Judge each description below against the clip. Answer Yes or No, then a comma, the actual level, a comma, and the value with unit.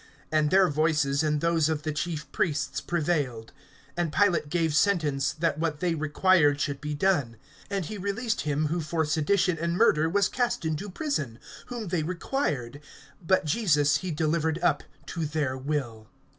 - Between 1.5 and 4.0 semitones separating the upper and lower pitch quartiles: Yes, average, 3.2 semitones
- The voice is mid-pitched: Yes, medium, 155 Hz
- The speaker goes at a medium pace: Yes, average, 165 wpm